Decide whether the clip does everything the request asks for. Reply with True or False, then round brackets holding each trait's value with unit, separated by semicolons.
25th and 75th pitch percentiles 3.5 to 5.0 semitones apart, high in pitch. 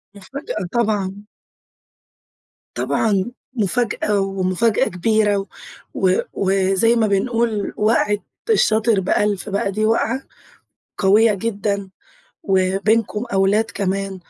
False (2.5 semitones; 205 Hz)